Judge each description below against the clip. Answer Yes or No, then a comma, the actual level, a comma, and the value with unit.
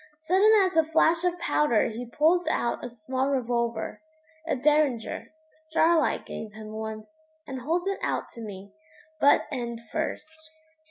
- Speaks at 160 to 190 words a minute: No, average, 150 wpm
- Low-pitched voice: No, very high, 275 Hz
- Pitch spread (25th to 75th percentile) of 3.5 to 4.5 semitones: No, wide, 5.5 semitones